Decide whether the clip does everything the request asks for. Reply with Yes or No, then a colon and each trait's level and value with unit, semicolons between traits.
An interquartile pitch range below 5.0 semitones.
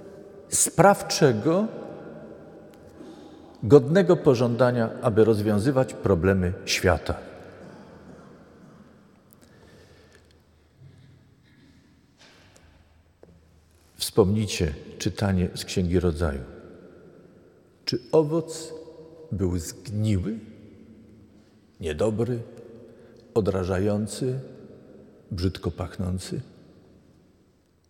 No: wide, 5.4 semitones